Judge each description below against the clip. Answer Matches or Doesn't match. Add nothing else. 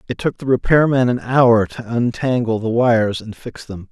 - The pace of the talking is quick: Matches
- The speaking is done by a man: Matches